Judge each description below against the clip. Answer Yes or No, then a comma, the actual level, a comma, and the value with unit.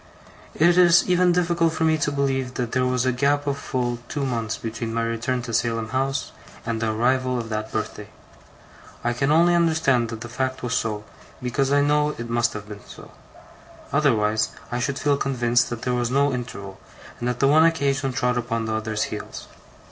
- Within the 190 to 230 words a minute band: Yes, average, 200 wpm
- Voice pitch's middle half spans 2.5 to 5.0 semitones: Yes, average, 3.6 semitones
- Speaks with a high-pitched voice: No, low, 125 Hz